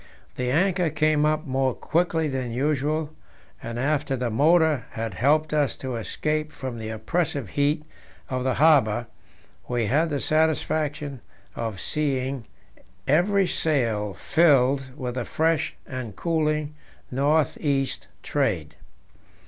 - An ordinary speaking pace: No, slow, 125 wpm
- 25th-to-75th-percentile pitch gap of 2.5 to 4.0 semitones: Yes, average, 3.6 semitones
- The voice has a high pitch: No, medium, 140 Hz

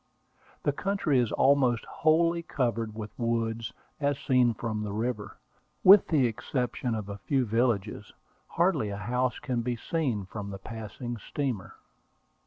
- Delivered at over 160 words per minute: No, average, 145 wpm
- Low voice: Yes, low, 120 Hz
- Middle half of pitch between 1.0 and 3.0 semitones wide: No, average, 3.8 semitones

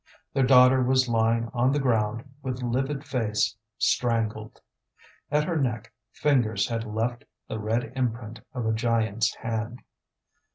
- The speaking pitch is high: No, low, 120 Hz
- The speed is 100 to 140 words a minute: Yes, slow, 135 wpm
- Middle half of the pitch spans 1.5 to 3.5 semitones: Yes, narrow, 2.4 semitones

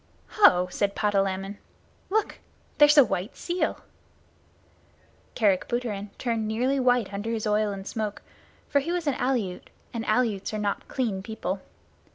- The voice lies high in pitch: Yes, high, 215 Hz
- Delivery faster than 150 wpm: No, average, 145 wpm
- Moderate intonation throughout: Yes, average, 4.1 semitones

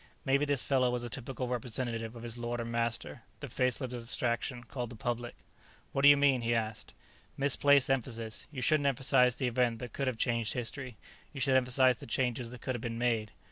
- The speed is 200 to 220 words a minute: Yes, fast, 205 wpm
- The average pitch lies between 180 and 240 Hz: No, low, 125 Hz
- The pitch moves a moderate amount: No, narrow, 2.1 semitones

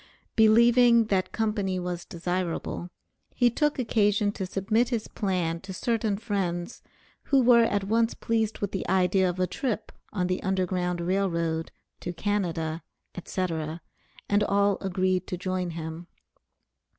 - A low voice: No, high, 190 Hz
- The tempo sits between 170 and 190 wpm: No, average, 140 wpm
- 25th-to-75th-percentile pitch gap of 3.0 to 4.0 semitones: Yes, average, 3.4 semitones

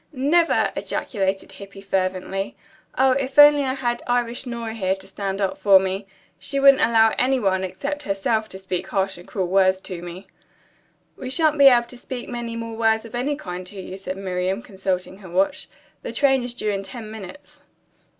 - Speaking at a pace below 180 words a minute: No, average, 190 wpm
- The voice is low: No, high, 210 Hz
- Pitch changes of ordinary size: Yes, average, 4.6 semitones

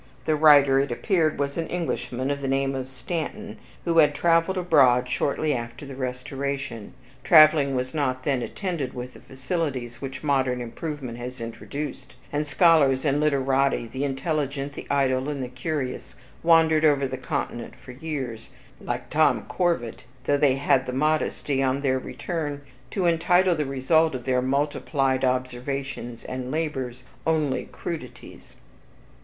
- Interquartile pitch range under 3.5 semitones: Yes, average, 3.1 semitones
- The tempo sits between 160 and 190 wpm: No, average, 150 wpm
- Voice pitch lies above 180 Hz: No, medium, 140 Hz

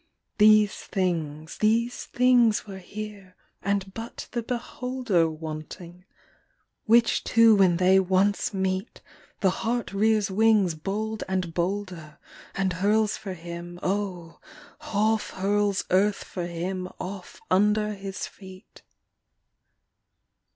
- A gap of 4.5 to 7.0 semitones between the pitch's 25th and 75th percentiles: No, average, 2.8 semitones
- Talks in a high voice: Yes, high, 195 Hz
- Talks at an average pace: No, slow, 110 wpm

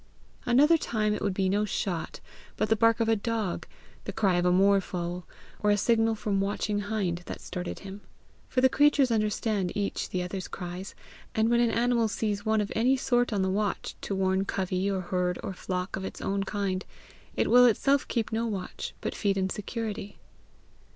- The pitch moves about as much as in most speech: Yes, average, 3.0 semitones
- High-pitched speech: Yes, high, 205 Hz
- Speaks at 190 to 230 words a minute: Yes, average, 195 wpm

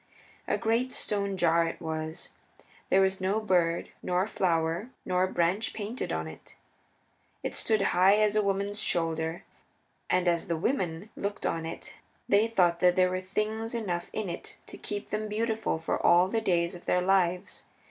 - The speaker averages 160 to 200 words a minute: Yes, average, 170 wpm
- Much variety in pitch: No, average, 3.7 semitones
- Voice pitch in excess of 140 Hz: Yes, medium, 185 Hz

